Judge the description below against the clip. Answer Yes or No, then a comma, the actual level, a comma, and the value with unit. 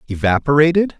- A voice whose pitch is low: No, medium, 145 Hz